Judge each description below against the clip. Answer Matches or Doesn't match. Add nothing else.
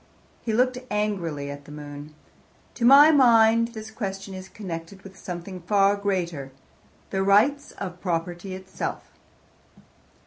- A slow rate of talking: Matches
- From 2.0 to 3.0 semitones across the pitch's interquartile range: Doesn't match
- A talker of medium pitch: Doesn't match